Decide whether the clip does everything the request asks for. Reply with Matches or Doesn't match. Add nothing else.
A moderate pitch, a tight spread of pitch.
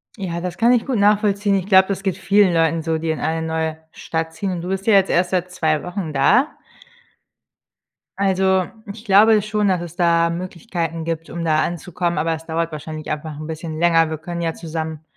Doesn't match